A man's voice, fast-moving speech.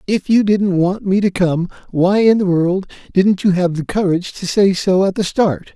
Yes: male; fast, 230 wpm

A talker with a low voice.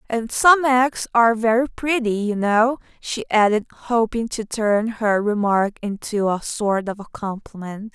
No: high, 220 Hz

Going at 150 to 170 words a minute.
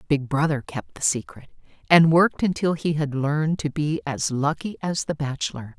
No: average, 185 wpm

